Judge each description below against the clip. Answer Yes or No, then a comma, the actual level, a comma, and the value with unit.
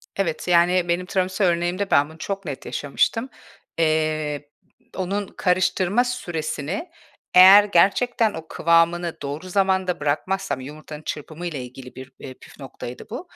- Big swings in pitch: No, average, 3.9 semitones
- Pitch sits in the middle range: Yes, medium, 175 Hz